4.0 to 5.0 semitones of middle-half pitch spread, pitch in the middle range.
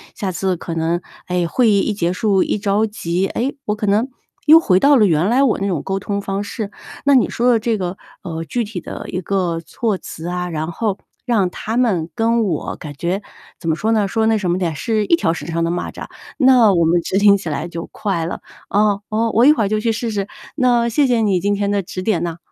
No: average, 4.3 semitones; high, 200 Hz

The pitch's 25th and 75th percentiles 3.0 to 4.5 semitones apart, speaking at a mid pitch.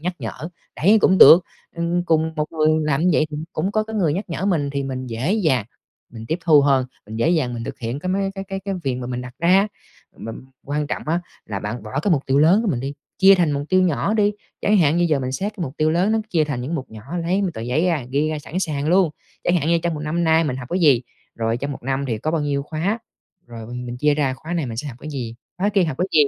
No: average, 5.1 semitones; medium, 155 Hz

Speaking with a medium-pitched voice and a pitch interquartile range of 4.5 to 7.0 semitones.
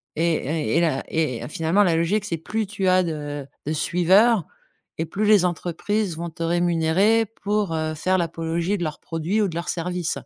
No: medium, 170 Hz; average, 3.2 semitones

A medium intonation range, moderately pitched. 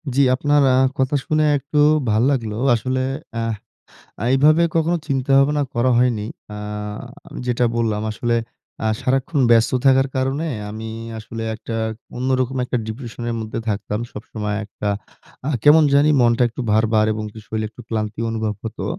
No: average, 3.6 semitones; low, 120 Hz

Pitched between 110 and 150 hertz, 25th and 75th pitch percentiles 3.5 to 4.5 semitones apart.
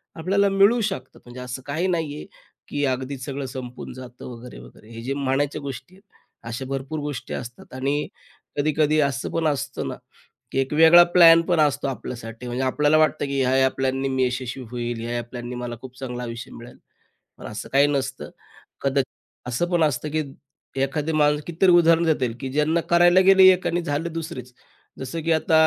Yes: medium, 140 Hz; average, 4.0 semitones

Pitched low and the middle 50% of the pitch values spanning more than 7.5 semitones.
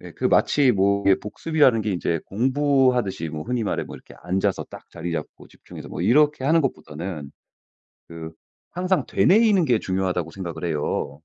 Yes: low, 100 Hz; wide, 7.9 semitones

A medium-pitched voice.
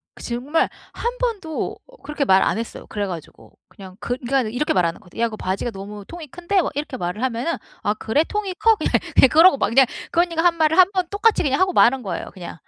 No: very high, 270 Hz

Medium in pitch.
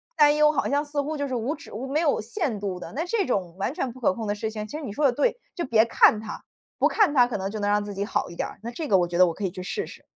No: high, 235 Hz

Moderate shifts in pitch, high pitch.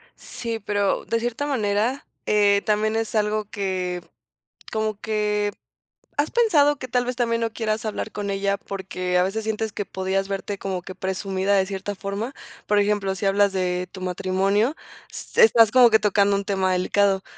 No: narrow, 2.3 semitones; high, 205 Hz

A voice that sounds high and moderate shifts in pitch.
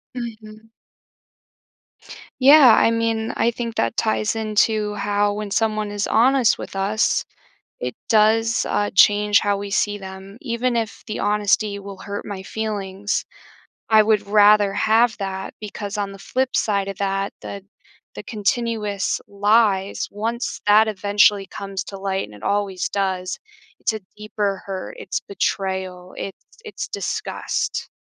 No: high, 205 Hz; narrow, 1.9 semitones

